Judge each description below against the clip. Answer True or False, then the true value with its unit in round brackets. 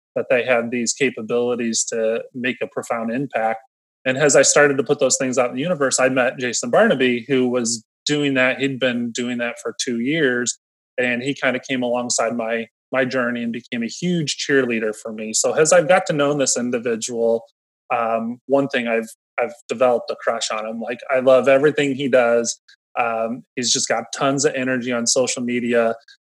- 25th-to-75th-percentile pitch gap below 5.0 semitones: True (2.8 semitones)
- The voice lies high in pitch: False (125 Hz)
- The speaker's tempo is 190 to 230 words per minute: True (200 wpm)